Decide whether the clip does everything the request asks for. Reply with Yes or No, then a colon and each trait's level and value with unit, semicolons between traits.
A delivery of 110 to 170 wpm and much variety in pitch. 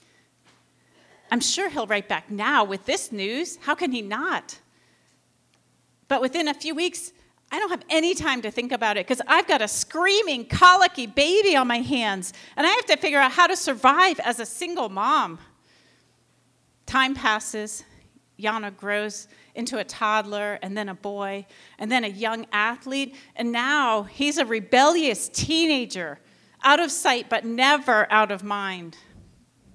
Yes: average, 160 wpm; wide, 6.3 semitones